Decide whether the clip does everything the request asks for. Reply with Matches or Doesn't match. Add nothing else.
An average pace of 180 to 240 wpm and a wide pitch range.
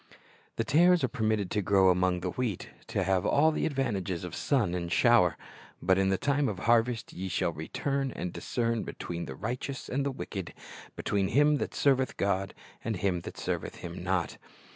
Matches